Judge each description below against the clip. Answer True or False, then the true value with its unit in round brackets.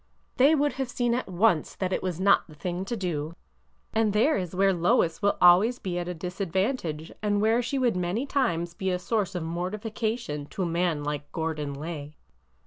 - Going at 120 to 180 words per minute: False (200 wpm)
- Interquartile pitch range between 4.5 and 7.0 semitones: True (4.8 semitones)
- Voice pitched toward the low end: False (185 Hz)